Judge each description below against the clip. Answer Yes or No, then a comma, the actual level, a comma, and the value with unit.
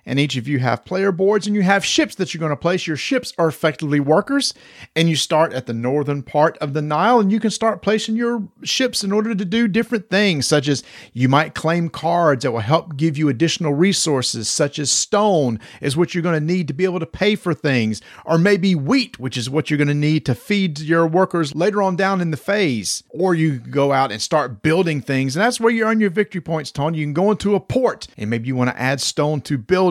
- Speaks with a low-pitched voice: No, medium, 160 Hz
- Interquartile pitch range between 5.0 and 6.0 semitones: Yes, wide, 5.5 semitones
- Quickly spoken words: Yes, fast, 250 wpm